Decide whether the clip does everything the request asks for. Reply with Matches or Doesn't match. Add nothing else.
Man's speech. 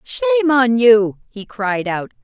Doesn't match